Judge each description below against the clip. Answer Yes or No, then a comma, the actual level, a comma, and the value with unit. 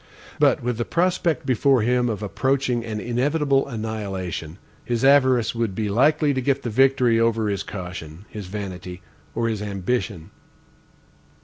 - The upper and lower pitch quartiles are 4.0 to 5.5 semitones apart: Yes, average, 4.4 semitones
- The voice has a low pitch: Yes, low, 115 Hz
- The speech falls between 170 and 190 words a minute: No, average, 145 wpm